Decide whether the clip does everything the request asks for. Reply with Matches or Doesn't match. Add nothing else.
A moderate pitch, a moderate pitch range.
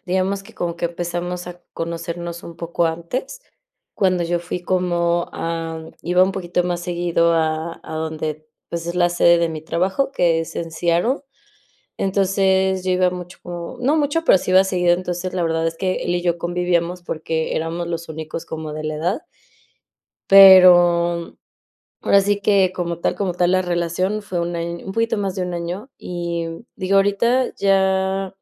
Doesn't match